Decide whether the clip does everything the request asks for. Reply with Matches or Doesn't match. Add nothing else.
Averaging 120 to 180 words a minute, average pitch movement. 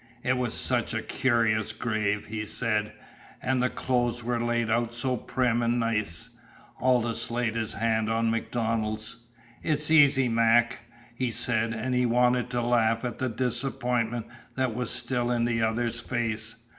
Doesn't match